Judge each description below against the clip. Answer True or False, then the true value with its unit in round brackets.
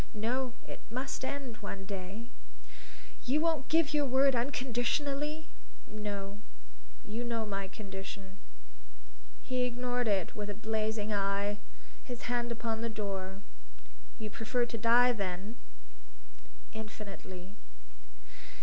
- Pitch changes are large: False (3.6 semitones)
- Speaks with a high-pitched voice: True (220 Hz)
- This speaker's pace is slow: True (115 wpm)